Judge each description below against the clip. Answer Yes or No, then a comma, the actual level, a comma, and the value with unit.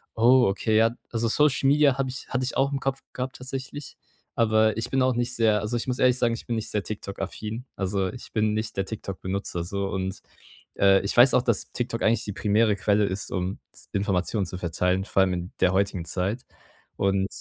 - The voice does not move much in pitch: No, average, 4.1 semitones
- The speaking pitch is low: Yes, low, 110 Hz